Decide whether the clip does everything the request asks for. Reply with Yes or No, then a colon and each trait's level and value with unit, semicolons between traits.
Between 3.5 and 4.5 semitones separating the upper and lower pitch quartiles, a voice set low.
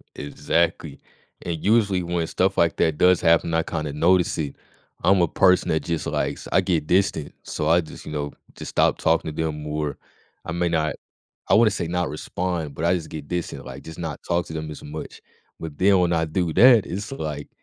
No: narrow, 2.5 semitones; very low, 85 Hz